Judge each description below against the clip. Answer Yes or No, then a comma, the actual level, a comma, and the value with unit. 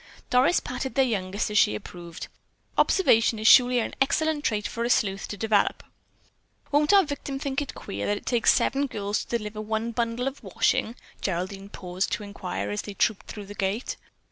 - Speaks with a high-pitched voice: Yes, high, 220 Hz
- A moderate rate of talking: Yes, average, 190 wpm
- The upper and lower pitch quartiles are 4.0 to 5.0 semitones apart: Yes, average, 4.7 semitones